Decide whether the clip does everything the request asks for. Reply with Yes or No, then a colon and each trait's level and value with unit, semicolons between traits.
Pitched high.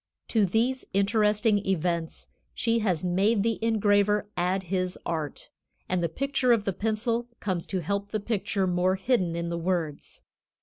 Yes: high, 200 Hz